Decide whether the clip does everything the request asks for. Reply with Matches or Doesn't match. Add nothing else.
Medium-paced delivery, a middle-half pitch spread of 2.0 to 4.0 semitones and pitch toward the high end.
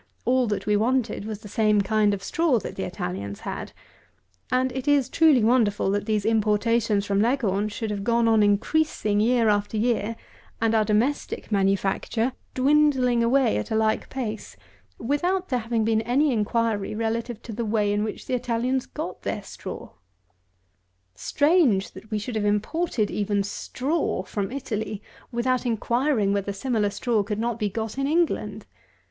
Matches